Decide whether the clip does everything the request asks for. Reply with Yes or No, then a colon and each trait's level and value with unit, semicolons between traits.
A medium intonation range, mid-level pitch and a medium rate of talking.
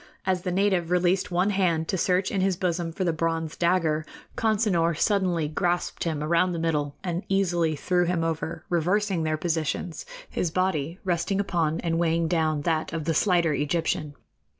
No: narrow, 2.2 semitones; medium, 170 Hz; average, 175 wpm